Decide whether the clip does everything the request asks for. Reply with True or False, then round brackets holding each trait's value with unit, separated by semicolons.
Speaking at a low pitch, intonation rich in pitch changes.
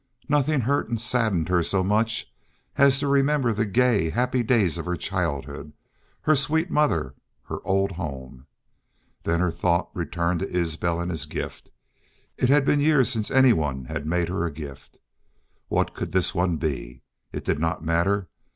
True (95 Hz; 7.4 semitones)